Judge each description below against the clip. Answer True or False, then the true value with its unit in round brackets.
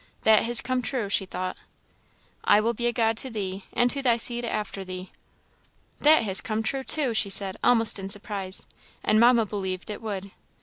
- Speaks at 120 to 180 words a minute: False (190 wpm)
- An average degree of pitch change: True (3.4 semitones)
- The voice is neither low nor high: False (220 Hz)